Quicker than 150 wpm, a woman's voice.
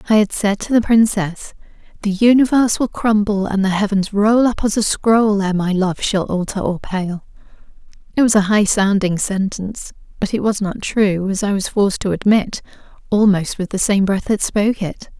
Yes: average, 195 wpm; female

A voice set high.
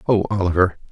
No: very low, 95 Hz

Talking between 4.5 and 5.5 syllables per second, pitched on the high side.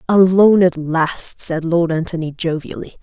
No: 4.7 syllables/s; medium, 170 Hz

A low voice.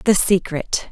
No: medium, 180 Hz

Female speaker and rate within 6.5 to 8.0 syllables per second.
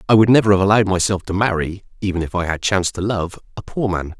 No: male; 6.7 syllables/s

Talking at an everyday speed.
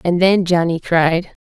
Yes: average, 170 wpm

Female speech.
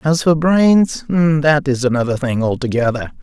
No: male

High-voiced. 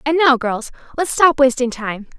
Yes: very high, 265 Hz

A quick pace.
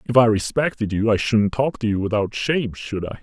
Yes: fast, 240 wpm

